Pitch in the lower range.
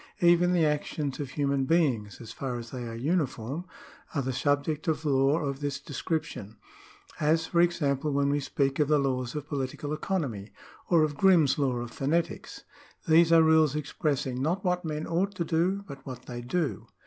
No: medium, 145 Hz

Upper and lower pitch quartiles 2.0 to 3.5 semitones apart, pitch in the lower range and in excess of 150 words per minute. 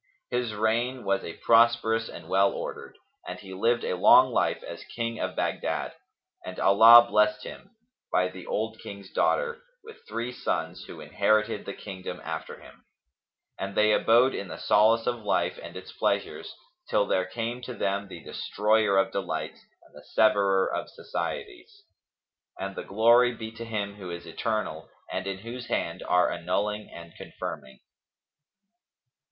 Yes: average, 3.2 semitones; low, 105 Hz; average, 160 wpm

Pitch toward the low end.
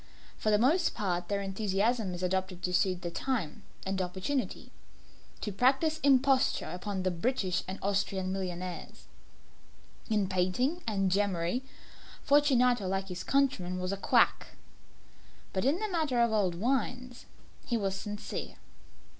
No: high, 200 Hz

